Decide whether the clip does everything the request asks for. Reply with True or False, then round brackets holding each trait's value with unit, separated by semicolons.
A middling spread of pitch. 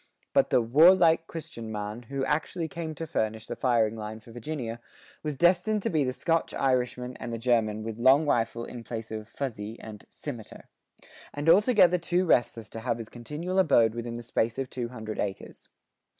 False (5.8 semitones)